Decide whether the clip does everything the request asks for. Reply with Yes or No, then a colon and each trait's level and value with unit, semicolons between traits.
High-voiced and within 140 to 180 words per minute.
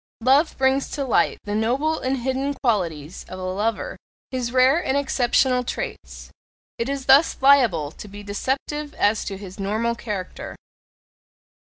Yes: high, 245 Hz; average, 150 wpm